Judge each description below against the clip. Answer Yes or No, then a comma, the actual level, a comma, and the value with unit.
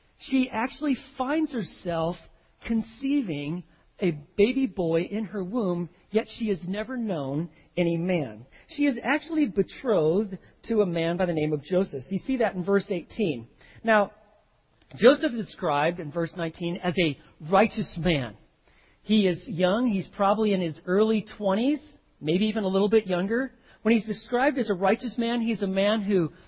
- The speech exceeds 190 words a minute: No, average, 165 wpm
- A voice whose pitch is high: Yes, high, 195 Hz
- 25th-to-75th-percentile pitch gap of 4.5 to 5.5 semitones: Yes, average, 5.0 semitones